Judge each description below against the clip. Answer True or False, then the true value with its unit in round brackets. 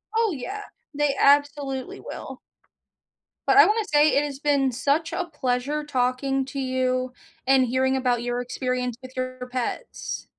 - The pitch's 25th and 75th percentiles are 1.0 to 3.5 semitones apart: True (2.5 semitones)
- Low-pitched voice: False (265 Hz)